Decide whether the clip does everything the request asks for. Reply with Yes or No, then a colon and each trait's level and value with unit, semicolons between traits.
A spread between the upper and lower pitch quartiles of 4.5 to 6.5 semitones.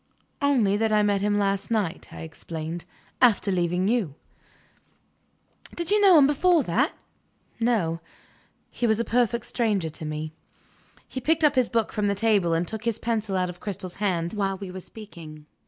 Yes: average, 5.0 semitones